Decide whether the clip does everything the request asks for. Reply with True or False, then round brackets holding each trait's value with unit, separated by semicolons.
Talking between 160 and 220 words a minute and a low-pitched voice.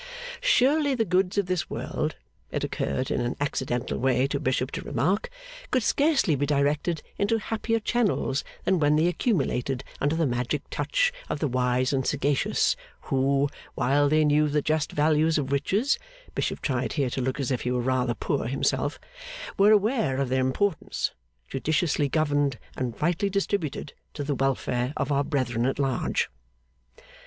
False (165 wpm; 145 Hz)